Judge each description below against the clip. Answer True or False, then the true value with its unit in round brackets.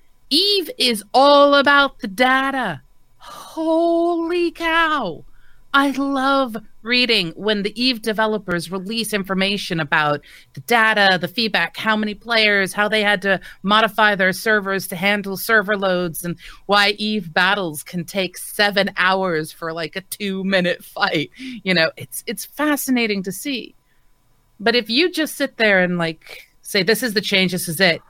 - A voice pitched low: False (210 Hz)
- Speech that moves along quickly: False (155 wpm)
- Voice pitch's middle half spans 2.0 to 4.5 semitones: False (4.9 semitones)